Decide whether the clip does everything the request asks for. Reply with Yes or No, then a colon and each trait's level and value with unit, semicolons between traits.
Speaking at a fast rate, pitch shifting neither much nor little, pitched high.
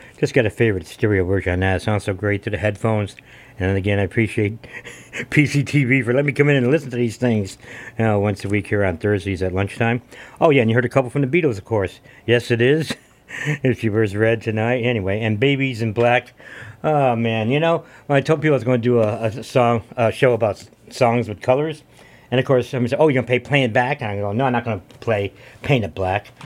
No: fast, 250 wpm; average, 3.8 semitones; low, 120 Hz